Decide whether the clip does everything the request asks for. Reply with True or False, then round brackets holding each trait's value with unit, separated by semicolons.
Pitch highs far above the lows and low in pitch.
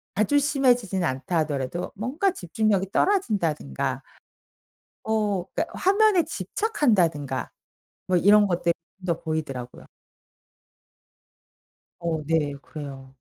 False (7.3 semitones; 185 Hz)